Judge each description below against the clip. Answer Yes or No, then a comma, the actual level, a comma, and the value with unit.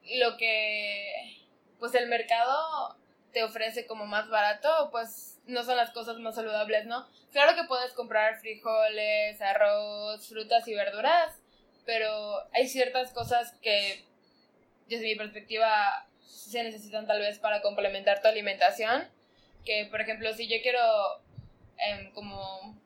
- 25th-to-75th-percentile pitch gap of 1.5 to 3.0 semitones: Yes, narrow, 2.5 semitones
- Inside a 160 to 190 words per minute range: No, average, 135 wpm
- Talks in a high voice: Yes, high, 225 Hz